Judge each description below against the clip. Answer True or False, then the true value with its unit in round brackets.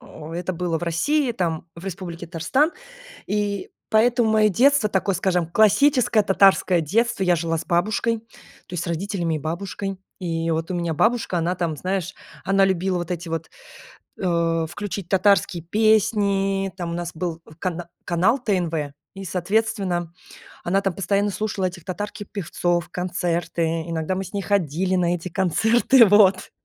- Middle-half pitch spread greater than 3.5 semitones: False (3.1 semitones)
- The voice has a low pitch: False (185 Hz)